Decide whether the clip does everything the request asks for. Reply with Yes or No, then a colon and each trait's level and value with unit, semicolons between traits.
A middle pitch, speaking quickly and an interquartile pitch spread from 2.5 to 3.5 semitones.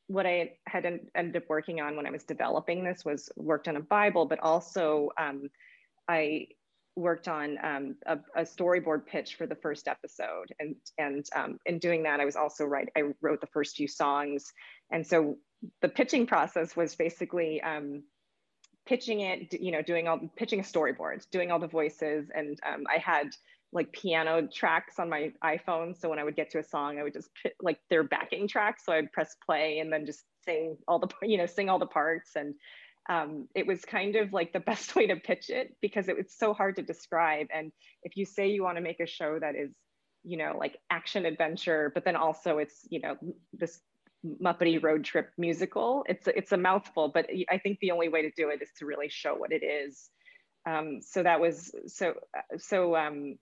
Yes: medium, 165 Hz; fast, 210 wpm; average, 3.1 semitones